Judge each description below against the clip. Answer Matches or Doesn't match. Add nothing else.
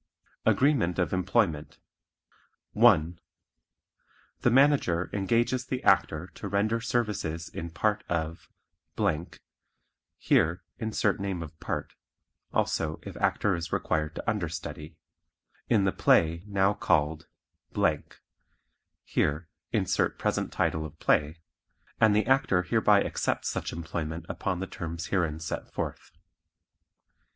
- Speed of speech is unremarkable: Doesn't match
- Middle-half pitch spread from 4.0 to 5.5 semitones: Matches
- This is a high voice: Doesn't match